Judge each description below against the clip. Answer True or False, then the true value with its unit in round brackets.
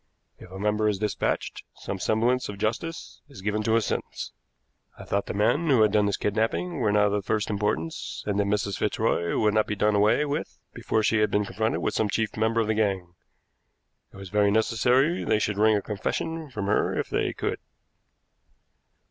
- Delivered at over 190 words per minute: True (205 wpm)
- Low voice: True (105 Hz)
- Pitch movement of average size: False (1.6 semitones)